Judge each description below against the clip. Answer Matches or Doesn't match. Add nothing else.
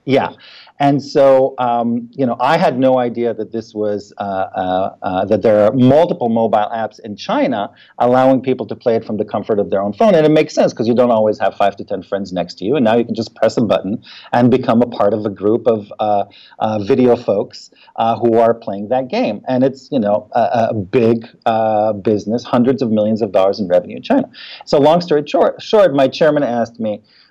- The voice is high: Doesn't match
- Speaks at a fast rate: Matches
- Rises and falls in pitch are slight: Doesn't match